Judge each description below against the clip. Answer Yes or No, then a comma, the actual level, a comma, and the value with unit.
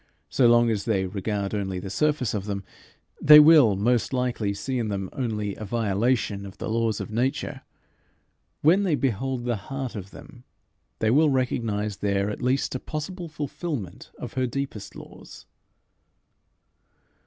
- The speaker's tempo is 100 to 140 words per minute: No, average, 155 wpm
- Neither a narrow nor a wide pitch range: Yes, average, 4.7 semitones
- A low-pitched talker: Yes, low, 115 Hz